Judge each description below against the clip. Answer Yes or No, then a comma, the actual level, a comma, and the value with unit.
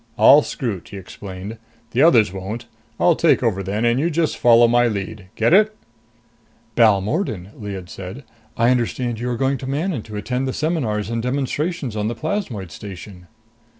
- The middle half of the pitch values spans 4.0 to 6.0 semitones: Yes, average, 4.8 semitones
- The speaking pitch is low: Yes, low, 115 Hz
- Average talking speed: Yes, average, 170 wpm